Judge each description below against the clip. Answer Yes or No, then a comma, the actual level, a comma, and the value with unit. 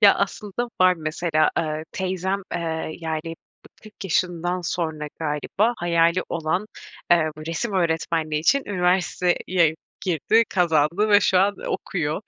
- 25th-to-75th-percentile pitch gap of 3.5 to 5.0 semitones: No, average, 2.9 semitones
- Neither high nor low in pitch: Yes, medium, 175 Hz